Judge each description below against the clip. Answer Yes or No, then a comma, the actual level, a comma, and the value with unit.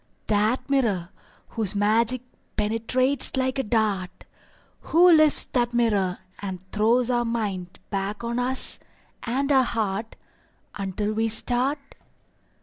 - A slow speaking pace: Yes, slow, 120 wpm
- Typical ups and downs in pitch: Yes, average, 3.6 semitones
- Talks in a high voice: Yes, high, 225 Hz